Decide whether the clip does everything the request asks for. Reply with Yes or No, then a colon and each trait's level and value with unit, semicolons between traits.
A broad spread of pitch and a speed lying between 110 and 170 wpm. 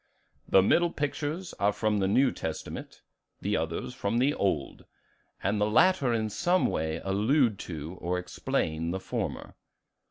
Yes: wide, 7.2 semitones; average, 150 wpm